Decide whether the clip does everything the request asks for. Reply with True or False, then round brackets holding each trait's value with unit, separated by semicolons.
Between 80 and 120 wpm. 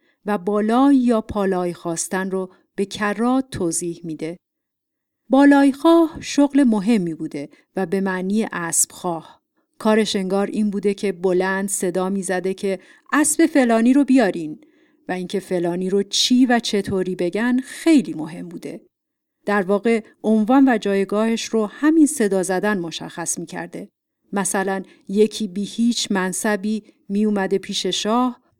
False (130 wpm)